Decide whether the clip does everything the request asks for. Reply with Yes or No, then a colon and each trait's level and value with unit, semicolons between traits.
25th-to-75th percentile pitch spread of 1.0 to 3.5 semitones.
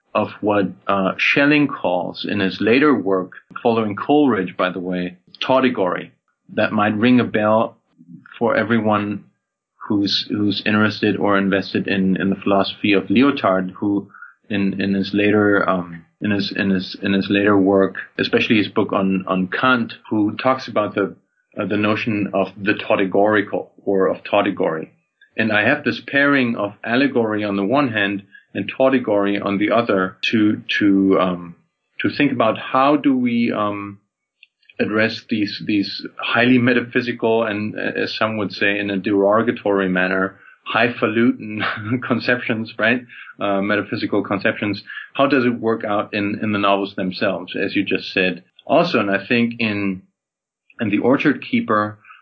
Yes: average, 2.7 semitones